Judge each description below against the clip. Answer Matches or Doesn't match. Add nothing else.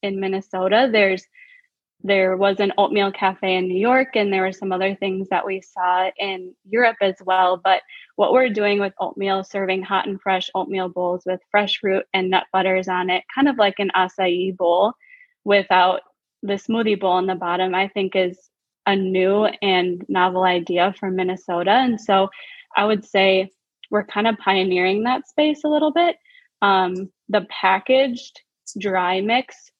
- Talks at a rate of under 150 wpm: Doesn't match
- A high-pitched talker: Matches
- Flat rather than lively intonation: Matches